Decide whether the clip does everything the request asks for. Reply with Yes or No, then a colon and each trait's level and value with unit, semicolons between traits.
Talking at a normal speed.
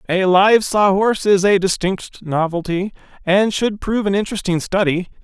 Yes: average, 160 wpm